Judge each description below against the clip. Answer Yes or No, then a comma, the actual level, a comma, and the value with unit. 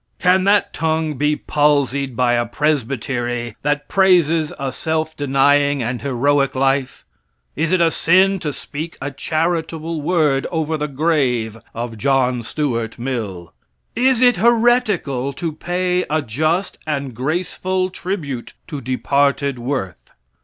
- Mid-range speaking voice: Yes, medium, 145 Hz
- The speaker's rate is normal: No, slow, 130 wpm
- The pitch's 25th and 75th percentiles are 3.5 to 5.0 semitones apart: Yes, average, 4.2 semitones